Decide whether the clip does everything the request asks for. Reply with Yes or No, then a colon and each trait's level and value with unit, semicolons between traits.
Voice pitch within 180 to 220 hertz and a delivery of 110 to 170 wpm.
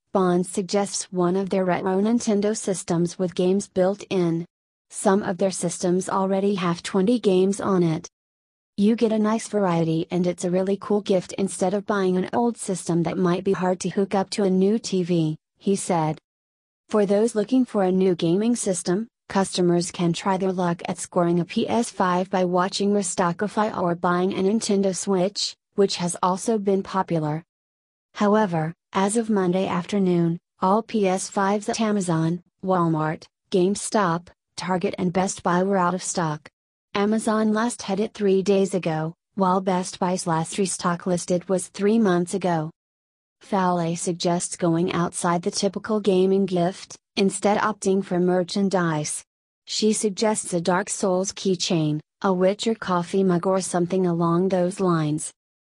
Yes: medium, 185 Hz; average, 155 wpm